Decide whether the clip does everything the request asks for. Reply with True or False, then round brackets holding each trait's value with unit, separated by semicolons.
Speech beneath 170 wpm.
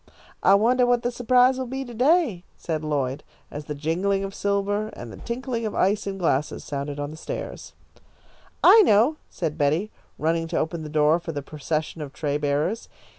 False (185 wpm)